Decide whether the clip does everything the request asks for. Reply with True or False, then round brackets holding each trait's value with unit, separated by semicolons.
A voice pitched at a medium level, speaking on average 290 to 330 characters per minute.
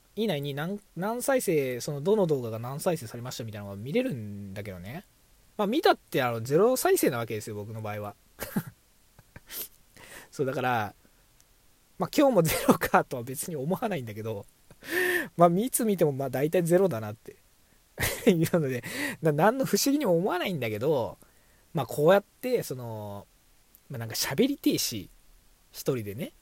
True (150 Hz; 320 characters per minute)